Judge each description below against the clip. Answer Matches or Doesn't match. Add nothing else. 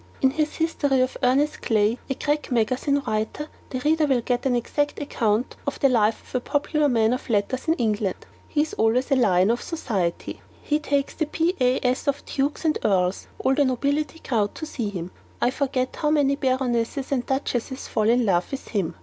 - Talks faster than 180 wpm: Matches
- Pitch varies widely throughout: Doesn't match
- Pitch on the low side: Doesn't match